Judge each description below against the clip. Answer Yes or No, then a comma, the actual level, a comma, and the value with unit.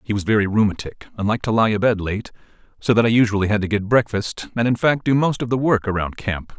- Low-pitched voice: Yes, low, 110 Hz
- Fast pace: Yes, fast, 255 wpm